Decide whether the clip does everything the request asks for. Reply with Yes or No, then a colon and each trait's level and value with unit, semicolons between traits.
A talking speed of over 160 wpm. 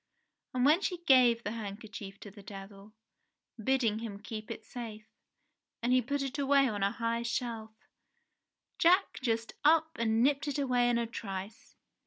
Yes: average, 170 wpm